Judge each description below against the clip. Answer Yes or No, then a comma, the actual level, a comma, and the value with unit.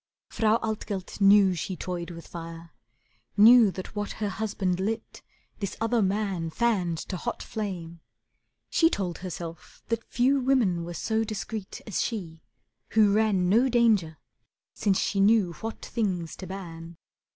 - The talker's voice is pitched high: Yes, high, 200 Hz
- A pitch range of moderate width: Yes, average, 4.0 semitones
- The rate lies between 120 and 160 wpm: Yes, average, 145 wpm